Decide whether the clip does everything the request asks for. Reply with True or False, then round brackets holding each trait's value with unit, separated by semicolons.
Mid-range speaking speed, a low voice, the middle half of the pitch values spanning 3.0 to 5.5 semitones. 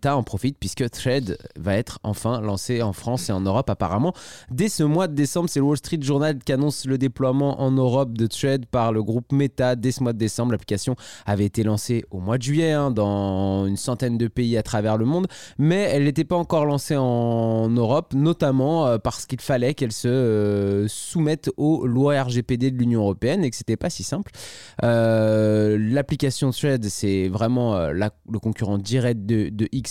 True (200 wpm; 125 Hz; 4.3 semitones)